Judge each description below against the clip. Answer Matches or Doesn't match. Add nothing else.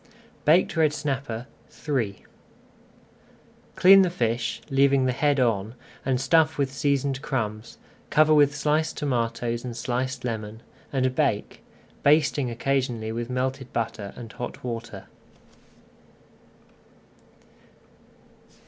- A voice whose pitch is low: Matches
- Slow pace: Matches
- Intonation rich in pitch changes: Doesn't match